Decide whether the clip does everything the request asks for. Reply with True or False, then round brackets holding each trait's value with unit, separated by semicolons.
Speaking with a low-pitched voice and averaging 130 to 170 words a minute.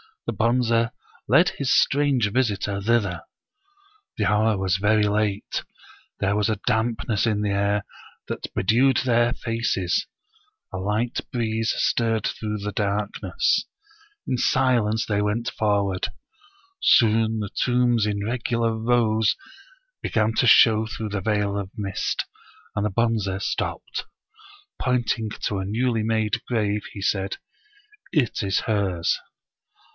True (110 Hz; 135 wpm)